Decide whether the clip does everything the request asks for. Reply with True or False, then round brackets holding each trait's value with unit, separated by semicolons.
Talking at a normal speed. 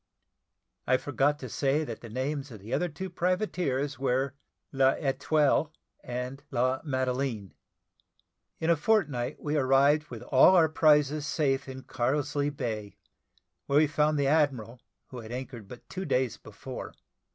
True (145 wpm)